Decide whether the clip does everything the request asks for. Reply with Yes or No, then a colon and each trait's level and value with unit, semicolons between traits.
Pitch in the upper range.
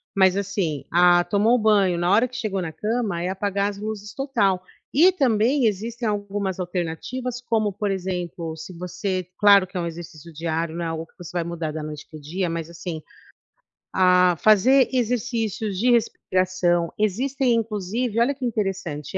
Yes: high, 195 Hz